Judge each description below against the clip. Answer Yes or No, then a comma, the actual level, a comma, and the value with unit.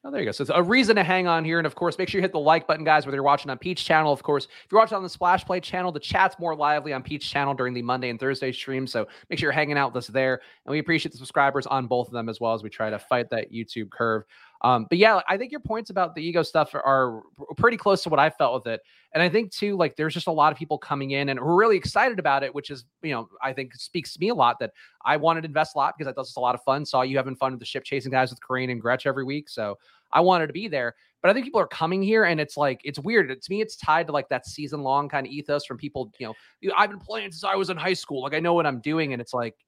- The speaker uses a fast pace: Yes, fast, 325 wpm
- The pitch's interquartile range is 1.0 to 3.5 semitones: No, average, 4.6 semitones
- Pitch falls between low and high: Yes, medium, 145 Hz